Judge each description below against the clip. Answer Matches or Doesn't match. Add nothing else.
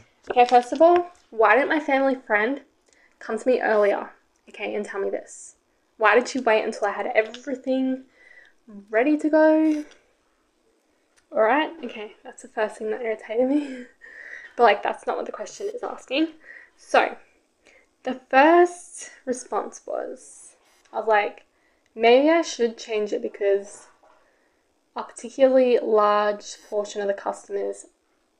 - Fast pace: Doesn't match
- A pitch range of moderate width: Doesn't match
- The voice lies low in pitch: Doesn't match